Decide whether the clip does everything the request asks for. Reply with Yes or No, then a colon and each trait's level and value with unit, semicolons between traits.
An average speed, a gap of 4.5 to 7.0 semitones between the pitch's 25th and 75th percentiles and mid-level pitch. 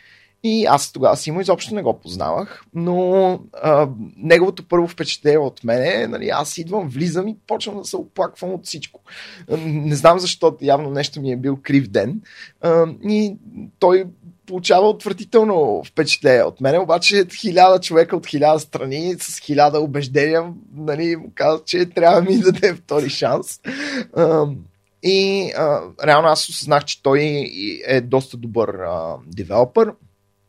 Yes: average, 150 wpm; average, 4.8 semitones; medium, 170 Hz